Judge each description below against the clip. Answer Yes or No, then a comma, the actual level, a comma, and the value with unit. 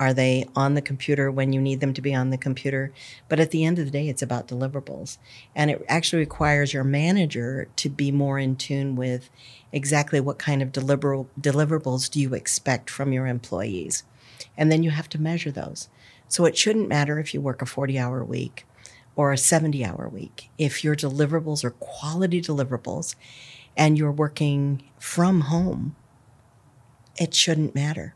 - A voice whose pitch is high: No, medium, 140 Hz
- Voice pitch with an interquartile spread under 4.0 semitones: Yes, average, 2.7 semitones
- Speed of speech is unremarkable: Yes, average, 180 wpm